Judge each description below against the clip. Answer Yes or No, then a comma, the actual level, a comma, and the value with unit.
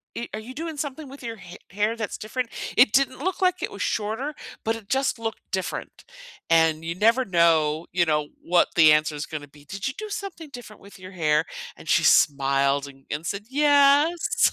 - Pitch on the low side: No, high, 210 Hz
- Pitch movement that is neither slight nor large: No, wide, 8.9 semitones